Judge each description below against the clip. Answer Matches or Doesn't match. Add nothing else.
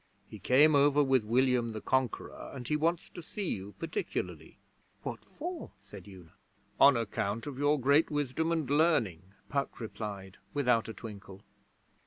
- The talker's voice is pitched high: Doesn't match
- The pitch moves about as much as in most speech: Doesn't match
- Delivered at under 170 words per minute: Matches